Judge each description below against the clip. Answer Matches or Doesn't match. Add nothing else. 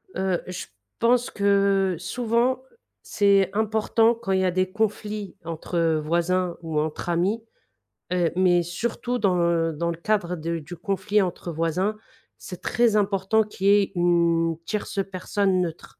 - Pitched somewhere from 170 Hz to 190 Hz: Matches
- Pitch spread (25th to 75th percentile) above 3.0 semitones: Matches